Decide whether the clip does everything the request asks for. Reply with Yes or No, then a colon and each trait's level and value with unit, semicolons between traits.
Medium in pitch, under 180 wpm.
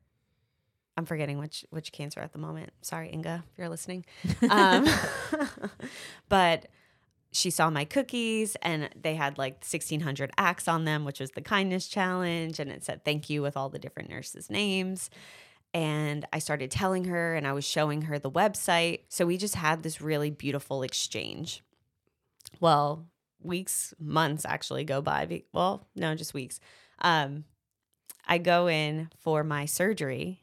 Yes: medium, 160 Hz; average, 160 wpm